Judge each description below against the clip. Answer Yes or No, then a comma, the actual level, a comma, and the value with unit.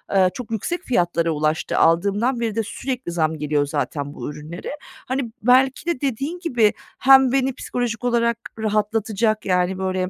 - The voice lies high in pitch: Yes, high, 220 Hz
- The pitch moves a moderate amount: No, wide, 6.3 semitones